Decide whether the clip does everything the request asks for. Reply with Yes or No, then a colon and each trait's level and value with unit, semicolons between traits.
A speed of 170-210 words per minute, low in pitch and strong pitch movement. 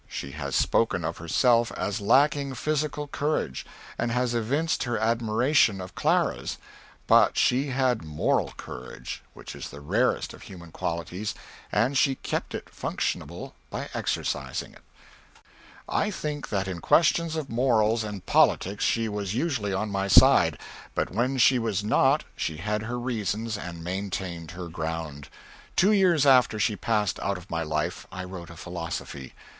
No: average, 155 wpm; low, 105 Hz; wide, 6.2 semitones